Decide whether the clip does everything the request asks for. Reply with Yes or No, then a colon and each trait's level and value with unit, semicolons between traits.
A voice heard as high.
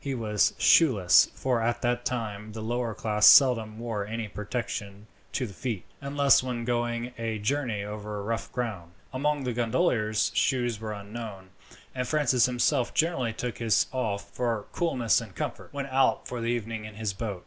No: low, 115 Hz